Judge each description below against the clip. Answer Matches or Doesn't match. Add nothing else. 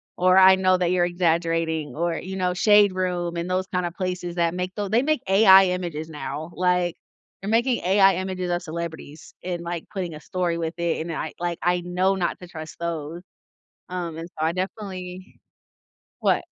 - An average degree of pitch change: Doesn't match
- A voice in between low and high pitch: Matches